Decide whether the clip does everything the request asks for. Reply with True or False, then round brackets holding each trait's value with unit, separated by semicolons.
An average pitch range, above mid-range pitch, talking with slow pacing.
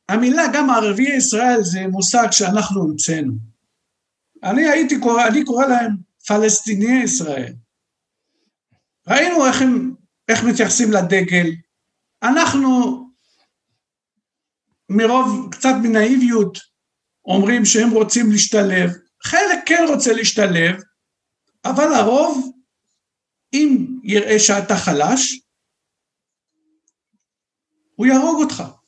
True (4.4 semitones; 235 Hz; 90 wpm)